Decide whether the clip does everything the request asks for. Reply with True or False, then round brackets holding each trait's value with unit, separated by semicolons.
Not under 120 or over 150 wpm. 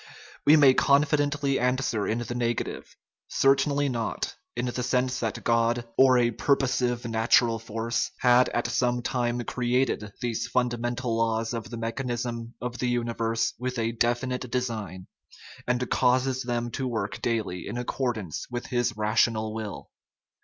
True (145 wpm)